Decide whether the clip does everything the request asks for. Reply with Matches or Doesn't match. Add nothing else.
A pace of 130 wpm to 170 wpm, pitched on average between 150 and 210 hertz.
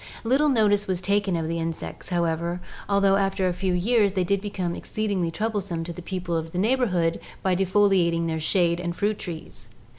Doesn't match